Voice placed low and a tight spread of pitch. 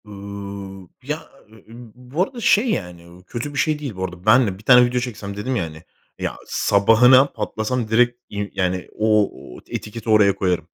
No: low, 110 Hz; average, 4.1 semitones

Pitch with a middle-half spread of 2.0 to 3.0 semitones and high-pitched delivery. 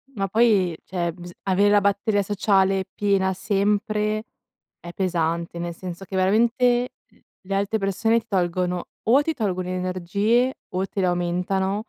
Yes: narrow, 2.5 semitones; high, 195 Hz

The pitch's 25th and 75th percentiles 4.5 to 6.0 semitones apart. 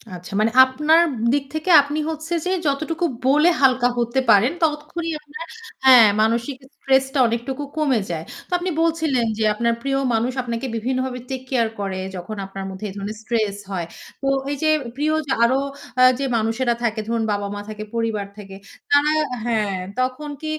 Yes: average, 5.0 semitones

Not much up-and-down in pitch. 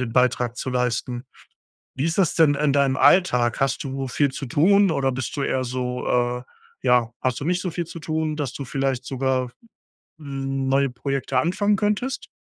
No: average, 3.7 semitones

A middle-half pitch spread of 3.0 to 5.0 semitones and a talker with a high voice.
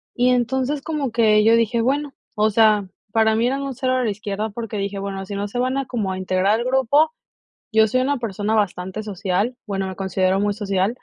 Yes: average, 4.0 semitones; high, 220 Hz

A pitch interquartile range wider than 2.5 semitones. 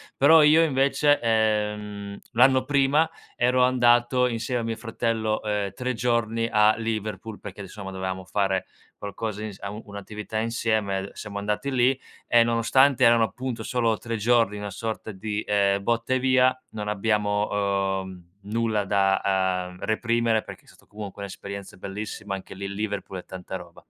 Yes: average, 2.9 semitones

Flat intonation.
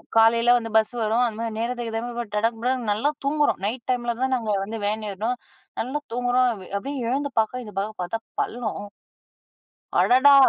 Yes: narrow, 2.3 semitones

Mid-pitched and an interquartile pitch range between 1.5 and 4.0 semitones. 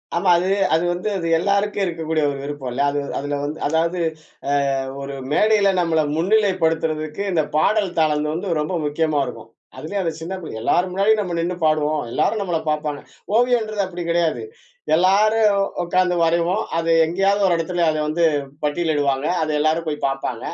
Yes: medium, 170 Hz; average, 3.7 semitones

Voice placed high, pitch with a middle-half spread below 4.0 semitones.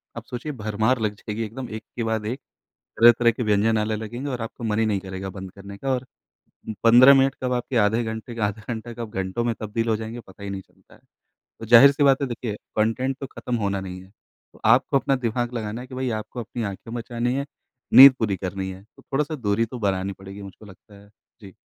No: low, 110 Hz; average, 3.2 semitones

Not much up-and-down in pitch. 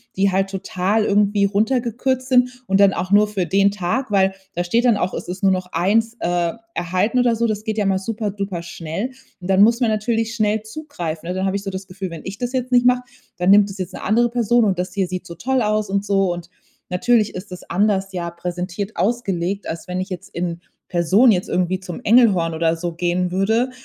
No: average, 3.5 semitones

